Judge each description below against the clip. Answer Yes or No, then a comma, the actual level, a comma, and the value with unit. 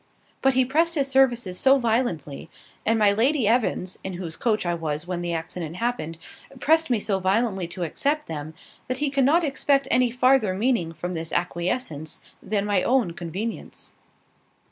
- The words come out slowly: No, average, 165 wpm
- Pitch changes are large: Yes, wide, 6.9 semitones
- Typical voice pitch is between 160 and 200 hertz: No, high, 215 Hz